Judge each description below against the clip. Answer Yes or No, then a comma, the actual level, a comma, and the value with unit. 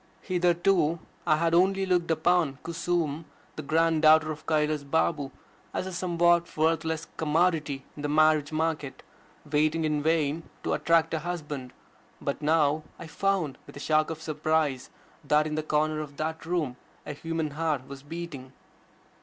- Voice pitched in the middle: Yes, medium, 155 Hz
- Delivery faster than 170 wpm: No, average, 155 wpm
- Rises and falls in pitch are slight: Yes, narrow, 1.9 semitones